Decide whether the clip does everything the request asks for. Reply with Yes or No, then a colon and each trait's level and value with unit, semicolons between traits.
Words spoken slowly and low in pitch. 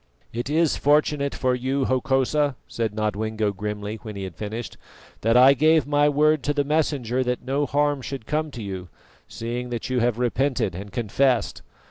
No: average, 175 wpm; low, 125 Hz